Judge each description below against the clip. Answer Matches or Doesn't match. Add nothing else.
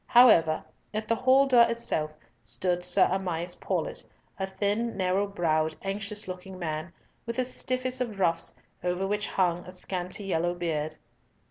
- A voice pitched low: Doesn't match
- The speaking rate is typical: Matches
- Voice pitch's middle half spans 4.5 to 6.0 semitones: Doesn't match